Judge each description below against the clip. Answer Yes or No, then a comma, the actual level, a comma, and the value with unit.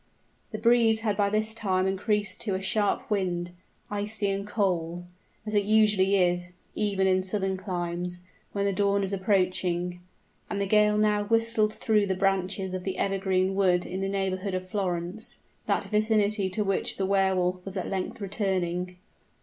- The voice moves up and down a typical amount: No, narrow, 2.0 semitones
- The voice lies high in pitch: Yes, high, 195 Hz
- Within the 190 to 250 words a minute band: No, average, 170 wpm